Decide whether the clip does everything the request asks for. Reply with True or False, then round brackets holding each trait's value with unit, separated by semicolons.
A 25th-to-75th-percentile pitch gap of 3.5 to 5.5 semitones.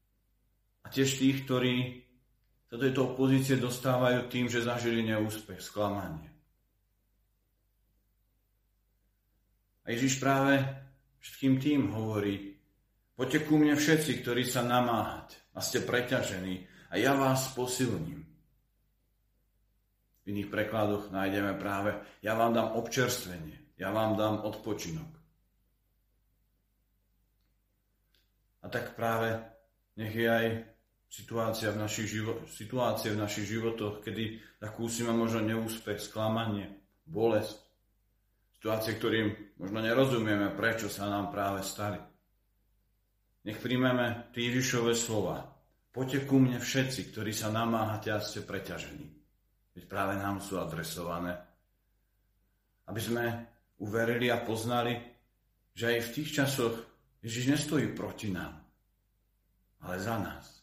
False (3.1 semitones)